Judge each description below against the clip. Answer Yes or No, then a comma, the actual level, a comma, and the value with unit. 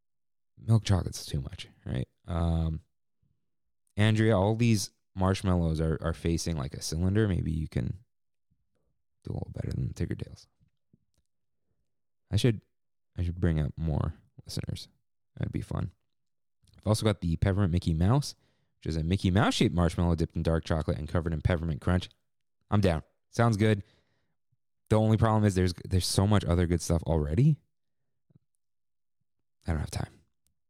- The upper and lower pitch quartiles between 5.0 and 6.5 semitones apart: No, average, 4.6 semitones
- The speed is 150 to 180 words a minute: Yes, average, 155 wpm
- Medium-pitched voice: No, very low, 95 Hz